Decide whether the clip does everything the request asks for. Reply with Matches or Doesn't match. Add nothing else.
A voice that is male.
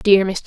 Doesn't match